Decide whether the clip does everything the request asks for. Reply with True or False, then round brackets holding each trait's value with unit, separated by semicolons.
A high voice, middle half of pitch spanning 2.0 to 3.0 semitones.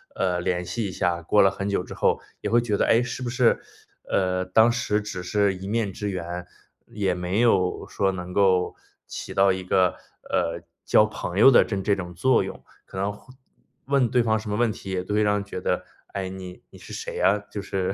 False (100 Hz; 2.7 semitones)